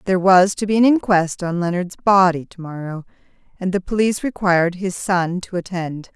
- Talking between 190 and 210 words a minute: No, average, 175 wpm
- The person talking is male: No, female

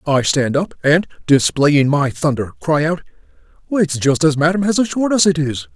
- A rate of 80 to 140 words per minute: No, average, 190 wpm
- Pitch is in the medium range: Yes, medium, 155 Hz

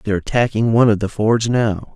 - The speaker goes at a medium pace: No, fast, 215 wpm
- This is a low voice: Yes, low, 110 Hz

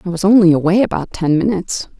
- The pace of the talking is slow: No, fast, 210 wpm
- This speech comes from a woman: Yes, female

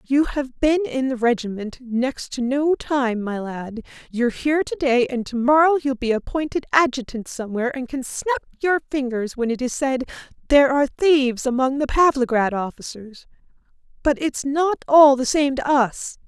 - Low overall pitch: No, very high, 265 Hz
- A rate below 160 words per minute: No, average, 170 wpm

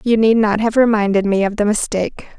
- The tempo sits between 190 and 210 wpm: No, fast, 225 wpm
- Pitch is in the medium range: No, high, 215 Hz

